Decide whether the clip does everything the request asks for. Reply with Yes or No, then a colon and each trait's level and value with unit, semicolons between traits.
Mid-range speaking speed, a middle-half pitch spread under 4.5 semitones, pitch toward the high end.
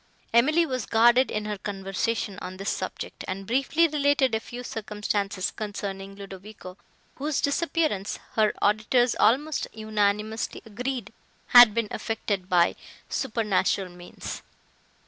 No: slow, 120 wpm; average, 4.0 semitones; high, 215 Hz